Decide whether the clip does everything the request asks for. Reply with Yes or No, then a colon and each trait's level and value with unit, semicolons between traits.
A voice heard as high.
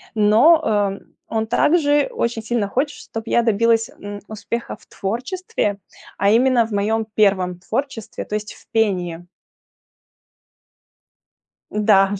Yes: high, 220 Hz